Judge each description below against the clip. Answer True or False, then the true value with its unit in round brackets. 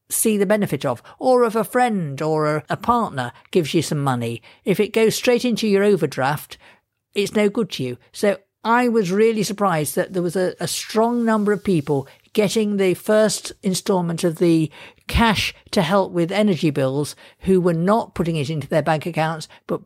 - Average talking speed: True (195 wpm)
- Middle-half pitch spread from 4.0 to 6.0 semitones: True (5.3 semitones)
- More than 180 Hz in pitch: True (190 Hz)